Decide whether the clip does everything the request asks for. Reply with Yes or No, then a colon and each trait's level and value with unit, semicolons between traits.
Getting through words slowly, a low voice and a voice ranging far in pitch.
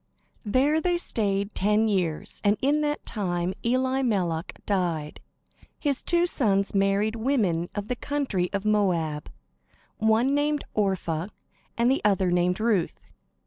No: slow, 125 wpm; high, 210 Hz; wide, 5.9 semitones